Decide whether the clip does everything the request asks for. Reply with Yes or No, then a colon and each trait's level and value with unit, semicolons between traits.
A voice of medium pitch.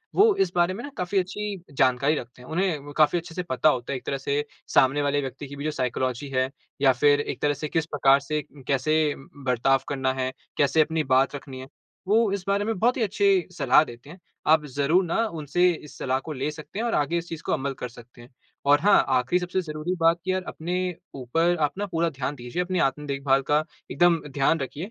Yes: medium, 150 Hz